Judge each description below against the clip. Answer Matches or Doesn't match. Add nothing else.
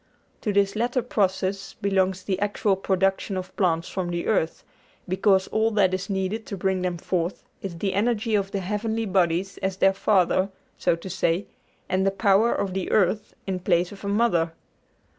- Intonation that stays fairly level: Matches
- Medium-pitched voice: Doesn't match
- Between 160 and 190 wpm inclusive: Matches